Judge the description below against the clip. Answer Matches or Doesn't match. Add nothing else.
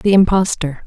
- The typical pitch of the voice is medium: Matches